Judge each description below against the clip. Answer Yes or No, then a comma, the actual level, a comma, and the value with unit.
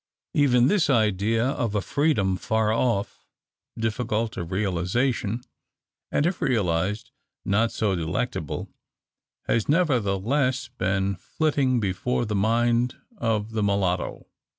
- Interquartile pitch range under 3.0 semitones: No, average, 4.1 semitones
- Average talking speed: No, slow, 110 wpm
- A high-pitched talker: No, low, 110 Hz